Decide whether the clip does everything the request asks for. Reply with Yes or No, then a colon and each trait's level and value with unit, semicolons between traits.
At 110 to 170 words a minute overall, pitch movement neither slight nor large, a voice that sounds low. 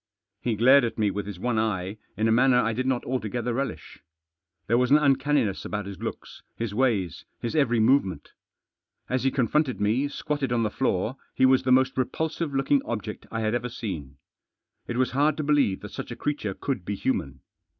No: average, 200 wpm; average, 4.0 semitones; low, 120 Hz